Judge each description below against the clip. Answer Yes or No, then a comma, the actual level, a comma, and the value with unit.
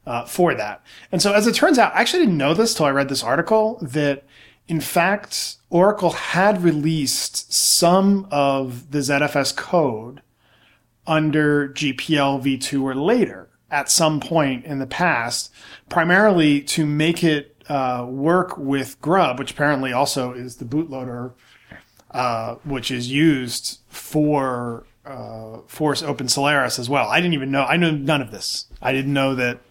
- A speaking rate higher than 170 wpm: No, average, 160 wpm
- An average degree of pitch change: Yes, average, 3.8 semitones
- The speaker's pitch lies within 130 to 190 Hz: Yes, medium, 140 Hz